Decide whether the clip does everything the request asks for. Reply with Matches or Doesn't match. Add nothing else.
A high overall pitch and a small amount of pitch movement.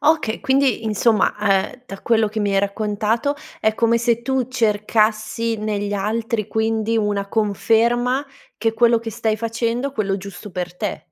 Matches